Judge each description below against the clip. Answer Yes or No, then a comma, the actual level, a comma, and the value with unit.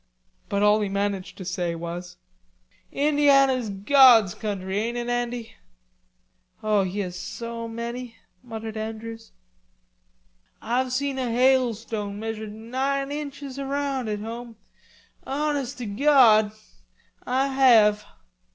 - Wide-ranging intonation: No, average, 4.0 semitones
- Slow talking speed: Yes, slow, 115 wpm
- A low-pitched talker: No, high, 230 Hz